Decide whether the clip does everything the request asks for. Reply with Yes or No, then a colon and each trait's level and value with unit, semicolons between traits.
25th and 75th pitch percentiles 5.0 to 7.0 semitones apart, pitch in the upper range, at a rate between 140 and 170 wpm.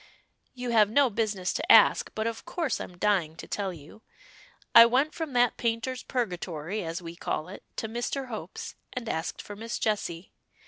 No: average, 5.3 semitones; high, 220 Hz; average, 180 wpm